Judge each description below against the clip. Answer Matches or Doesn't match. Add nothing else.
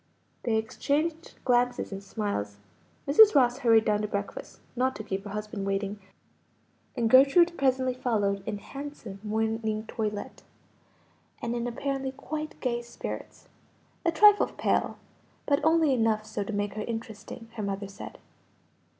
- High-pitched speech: Matches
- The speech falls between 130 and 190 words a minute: Matches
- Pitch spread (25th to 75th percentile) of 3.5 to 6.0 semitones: Matches